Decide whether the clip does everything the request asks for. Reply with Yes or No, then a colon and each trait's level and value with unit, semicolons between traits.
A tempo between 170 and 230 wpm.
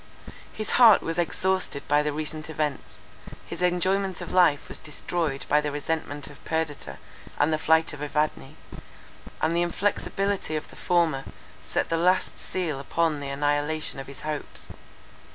No: average, 155 wpm